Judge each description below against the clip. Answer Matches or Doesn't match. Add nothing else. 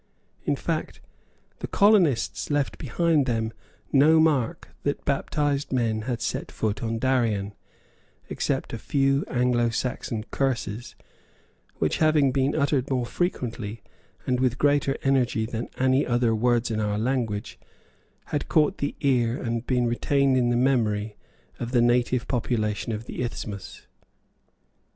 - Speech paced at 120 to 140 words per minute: Matches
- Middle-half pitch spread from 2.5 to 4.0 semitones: Matches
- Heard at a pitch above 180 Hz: Doesn't match